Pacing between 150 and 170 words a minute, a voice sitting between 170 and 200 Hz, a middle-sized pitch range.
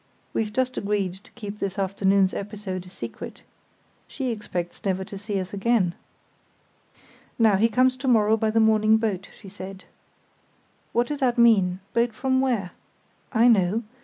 No: average, 160 wpm; high, 210 Hz; average, 3.3 semitones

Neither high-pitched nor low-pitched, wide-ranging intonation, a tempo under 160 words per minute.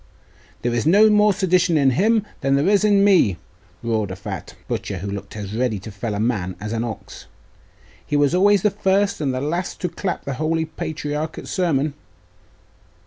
No: medium, 150 Hz; wide, 8.9 semitones; average, 195 wpm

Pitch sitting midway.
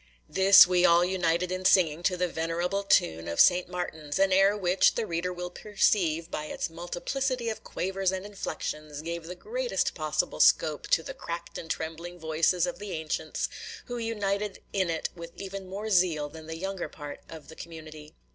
Yes: medium, 180 Hz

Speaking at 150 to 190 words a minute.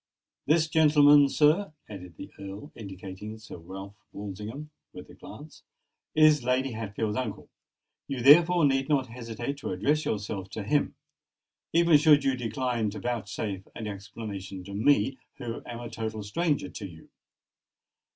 No: average, 140 wpm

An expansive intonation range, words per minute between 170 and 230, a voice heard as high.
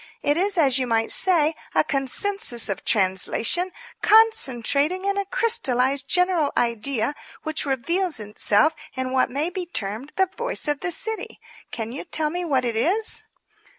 No: wide, 6.9 semitones; average, 155 wpm; very high, 295 Hz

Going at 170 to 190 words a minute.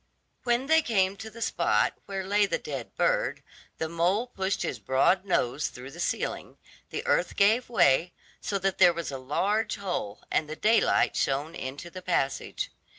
Yes: average, 175 wpm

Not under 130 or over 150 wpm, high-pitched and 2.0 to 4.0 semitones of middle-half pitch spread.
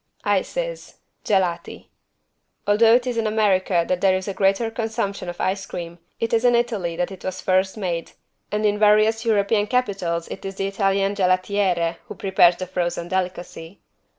No: average, 170 wpm; high, 195 Hz; average, 2.8 semitones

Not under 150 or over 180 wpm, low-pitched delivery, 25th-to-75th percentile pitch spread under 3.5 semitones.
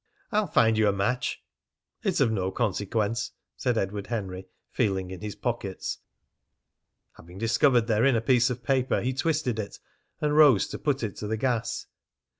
No: average, 165 wpm; low, 115 Hz; average, 3.8 semitones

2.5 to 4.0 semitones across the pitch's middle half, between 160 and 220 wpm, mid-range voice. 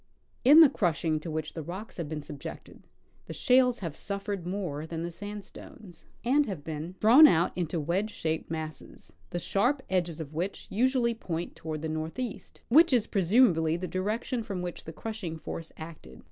No: wide, 5.6 semitones; average, 175 wpm; medium, 180 Hz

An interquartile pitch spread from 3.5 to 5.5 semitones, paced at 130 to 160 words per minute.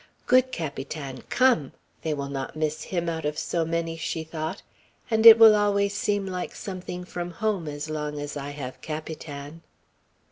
No: average, 4.5 semitones; average, 170 wpm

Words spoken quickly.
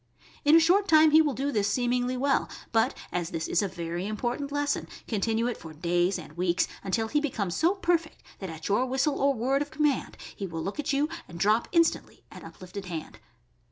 Yes: fast, 215 wpm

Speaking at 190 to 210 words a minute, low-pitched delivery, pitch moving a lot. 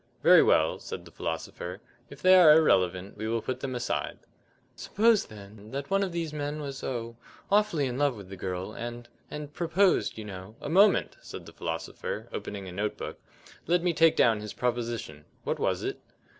Yes: average, 195 wpm; low, 120 Hz; wide, 7.6 semitones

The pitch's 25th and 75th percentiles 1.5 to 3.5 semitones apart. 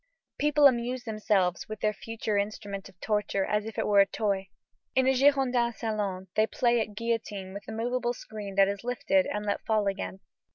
Yes: average, 3.0 semitones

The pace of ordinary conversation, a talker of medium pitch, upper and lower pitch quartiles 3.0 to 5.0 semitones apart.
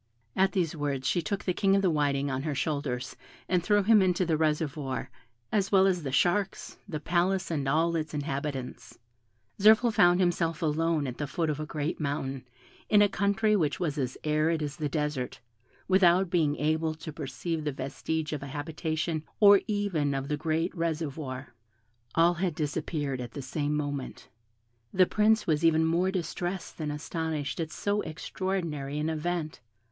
Yes: average, 175 wpm; medium, 160 Hz; average, 3.4 semitones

